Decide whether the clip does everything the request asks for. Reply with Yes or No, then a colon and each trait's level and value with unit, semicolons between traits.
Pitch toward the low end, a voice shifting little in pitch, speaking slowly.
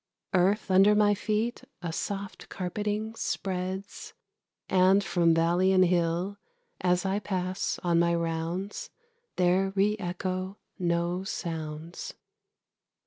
No: medium, 185 Hz; narrow, 2.3 semitones; slow, 110 wpm